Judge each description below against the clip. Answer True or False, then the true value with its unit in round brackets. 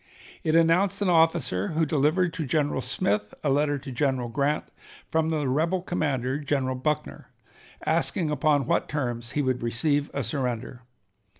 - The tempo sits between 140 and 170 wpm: True (155 wpm)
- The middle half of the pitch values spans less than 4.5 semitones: True (3.6 semitones)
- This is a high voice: False (145 Hz)